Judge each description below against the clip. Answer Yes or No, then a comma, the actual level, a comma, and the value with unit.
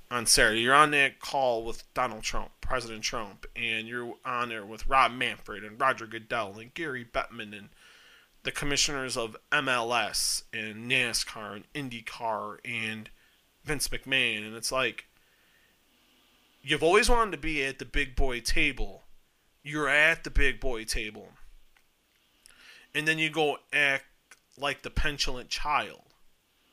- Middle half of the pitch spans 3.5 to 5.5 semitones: Yes, average, 4.3 semitones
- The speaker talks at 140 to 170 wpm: Yes, average, 145 wpm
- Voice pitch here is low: Yes, low, 130 Hz